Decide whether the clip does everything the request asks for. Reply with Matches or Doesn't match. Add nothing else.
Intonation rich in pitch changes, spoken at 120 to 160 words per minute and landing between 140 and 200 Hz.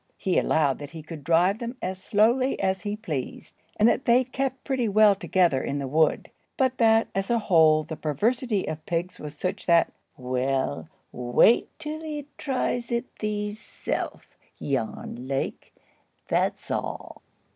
Matches